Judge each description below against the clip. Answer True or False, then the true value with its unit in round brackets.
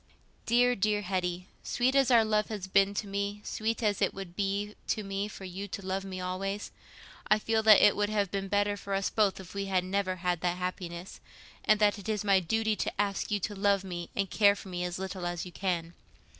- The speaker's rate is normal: False (230 wpm)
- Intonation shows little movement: True (2.0 semitones)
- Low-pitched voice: False (195 Hz)